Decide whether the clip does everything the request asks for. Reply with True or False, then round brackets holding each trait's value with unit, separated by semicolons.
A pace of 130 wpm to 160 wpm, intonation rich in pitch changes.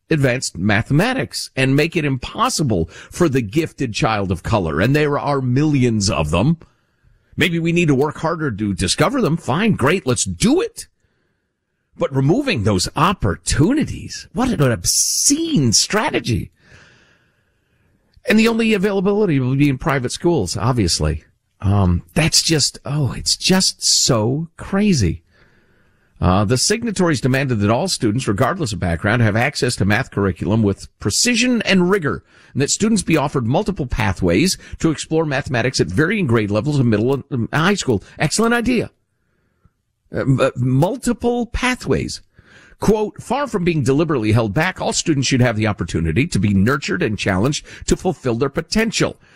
True (150 wpm; 7.6 semitones)